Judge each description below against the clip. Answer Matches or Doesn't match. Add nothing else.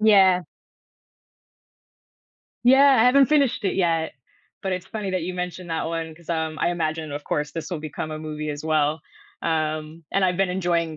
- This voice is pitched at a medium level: Matches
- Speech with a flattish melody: Doesn't match